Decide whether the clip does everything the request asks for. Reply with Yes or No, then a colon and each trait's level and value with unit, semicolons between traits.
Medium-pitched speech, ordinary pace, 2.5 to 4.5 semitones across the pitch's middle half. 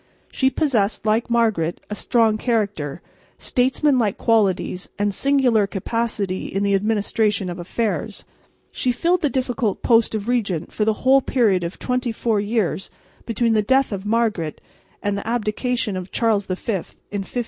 No: high, 220 Hz; average, 155 wpm; average, 3.3 semitones